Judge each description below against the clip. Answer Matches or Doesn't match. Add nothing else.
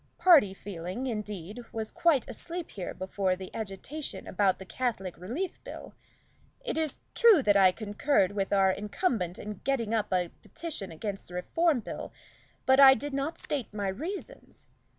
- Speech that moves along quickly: Doesn't match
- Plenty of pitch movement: Matches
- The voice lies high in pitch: Matches